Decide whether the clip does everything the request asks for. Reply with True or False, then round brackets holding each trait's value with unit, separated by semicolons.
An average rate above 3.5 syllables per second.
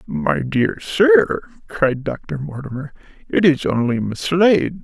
False (3.4 syllables/s)